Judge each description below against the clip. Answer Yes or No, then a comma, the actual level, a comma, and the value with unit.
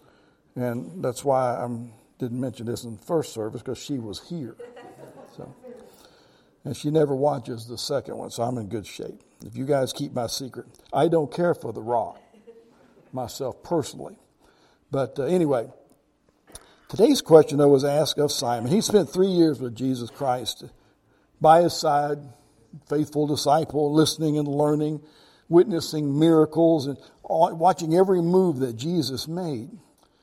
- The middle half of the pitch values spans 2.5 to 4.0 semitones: No, average, 4.7 semitones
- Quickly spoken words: No, average, 150 wpm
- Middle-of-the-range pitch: Yes, medium, 145 Hz